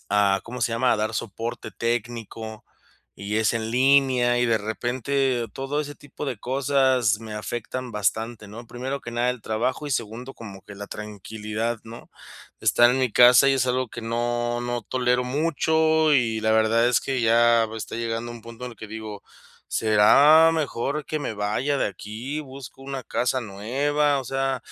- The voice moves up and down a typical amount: Yes, average, 3.2 semitones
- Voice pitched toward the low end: Yes, low, 120 Hz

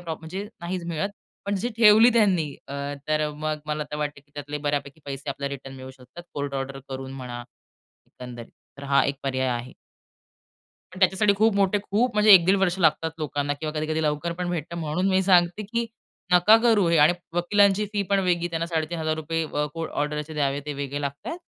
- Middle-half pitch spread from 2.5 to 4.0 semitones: No, average, 4.7 semitones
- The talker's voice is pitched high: No, medium, 160 Hz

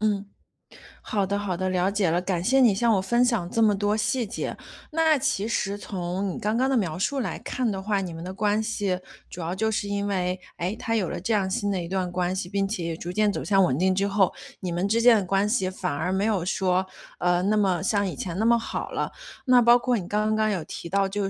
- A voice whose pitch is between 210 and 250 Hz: No, high, 200 Hz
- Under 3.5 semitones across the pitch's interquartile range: Yes, average, 2.8 semitones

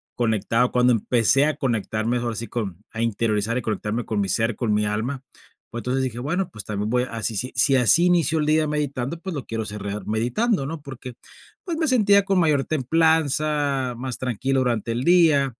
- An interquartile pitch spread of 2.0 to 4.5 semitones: No, average, 5.1 semitones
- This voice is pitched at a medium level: No, low, 125 Hz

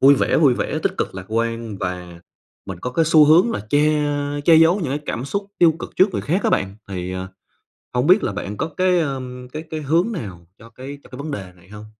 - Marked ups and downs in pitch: Yes, wide, 8.1 semitones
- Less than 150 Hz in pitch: Yes, low, 135 Hz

